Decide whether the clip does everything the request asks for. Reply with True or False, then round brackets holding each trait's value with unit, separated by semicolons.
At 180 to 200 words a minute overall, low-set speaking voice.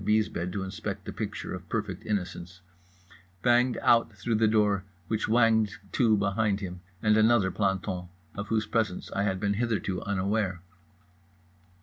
False (150 wpm; 105 Hz)